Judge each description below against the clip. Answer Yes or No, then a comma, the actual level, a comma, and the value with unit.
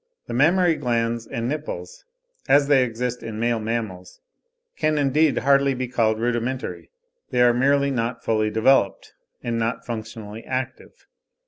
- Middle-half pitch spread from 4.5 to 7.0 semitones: No, average, 3.3 semitones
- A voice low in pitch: Yes, low, 120 Hz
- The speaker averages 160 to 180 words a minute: No, average, 140 wpm